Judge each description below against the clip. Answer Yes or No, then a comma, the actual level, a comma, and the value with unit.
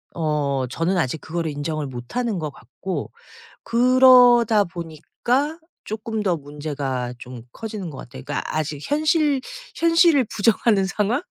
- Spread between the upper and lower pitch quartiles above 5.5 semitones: Yes, wide, 8.5 semitones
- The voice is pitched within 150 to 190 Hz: Yes, medium, 185 Hz